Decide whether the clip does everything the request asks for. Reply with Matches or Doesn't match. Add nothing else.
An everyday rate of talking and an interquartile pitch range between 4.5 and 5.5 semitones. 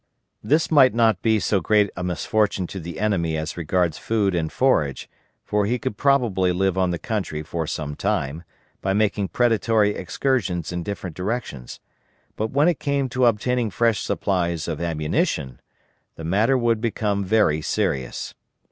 Matches